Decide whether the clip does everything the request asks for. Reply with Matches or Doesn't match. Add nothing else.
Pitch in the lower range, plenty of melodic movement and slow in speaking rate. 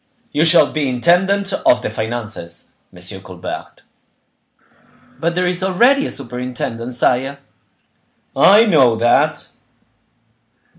Matches